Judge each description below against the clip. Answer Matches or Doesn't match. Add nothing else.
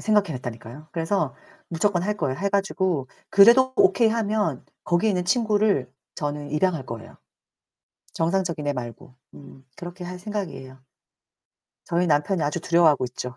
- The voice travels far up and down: Matches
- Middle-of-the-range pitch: Matches